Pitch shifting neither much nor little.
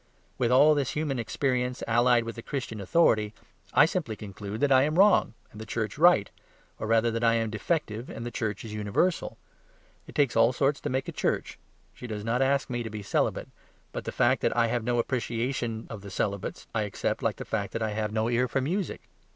Yes: average, 3.4 semitones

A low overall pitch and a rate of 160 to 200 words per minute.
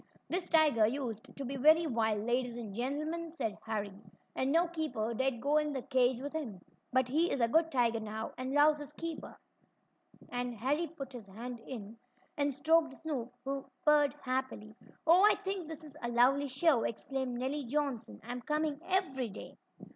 No: very high, 265 Hz; average, 180 wpm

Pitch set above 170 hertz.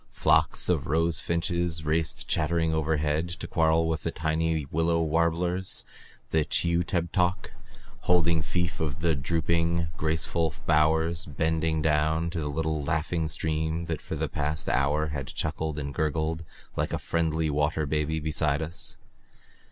No: very low, 80 Hz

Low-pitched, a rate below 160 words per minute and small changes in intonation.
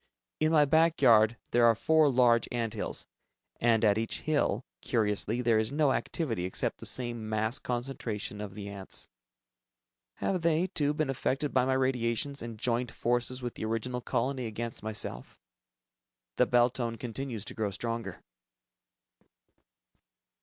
No: low, 120 Hz; average, 150 wpm; average, 3.3 semitones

